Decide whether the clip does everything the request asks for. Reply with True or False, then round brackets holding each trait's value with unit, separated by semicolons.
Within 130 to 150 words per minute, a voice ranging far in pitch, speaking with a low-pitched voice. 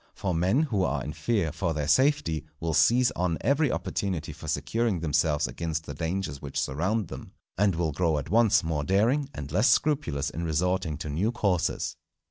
False (185 wpm; 5.8 semitones; 90 Hz)